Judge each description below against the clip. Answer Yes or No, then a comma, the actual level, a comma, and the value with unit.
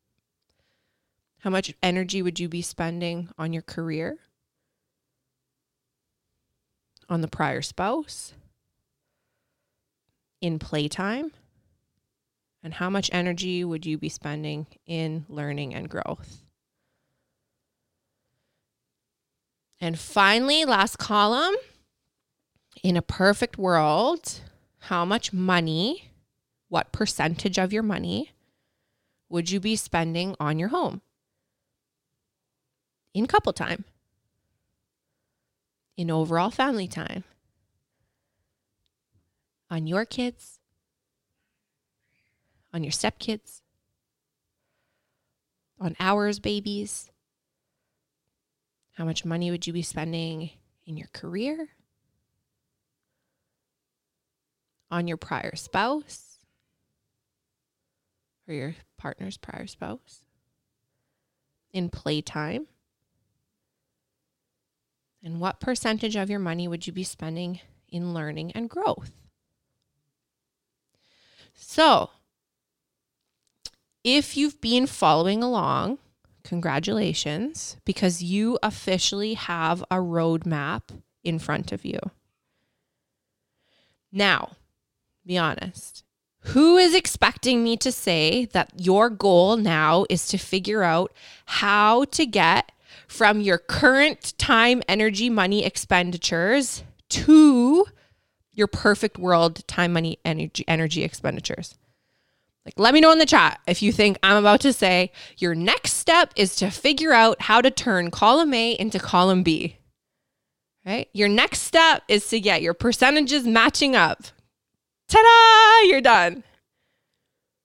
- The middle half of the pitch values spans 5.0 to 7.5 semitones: Yes, wide, 5.4 semitones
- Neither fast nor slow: No, slow, 100 wpm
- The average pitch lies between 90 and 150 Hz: No, medium, 185 Hz